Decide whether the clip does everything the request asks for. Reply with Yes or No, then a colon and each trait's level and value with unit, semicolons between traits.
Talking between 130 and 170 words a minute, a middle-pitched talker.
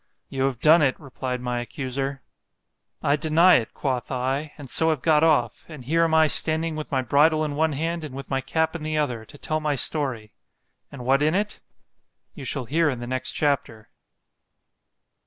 No: average, 195 wpm; medium, 145 Hz